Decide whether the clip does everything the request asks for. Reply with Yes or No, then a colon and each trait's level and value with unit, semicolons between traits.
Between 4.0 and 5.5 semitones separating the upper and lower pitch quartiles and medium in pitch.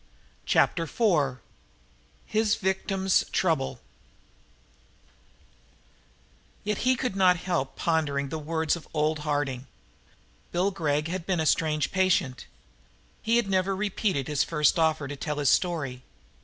Yes: average, 4.5 semitones; medium, 165 Hz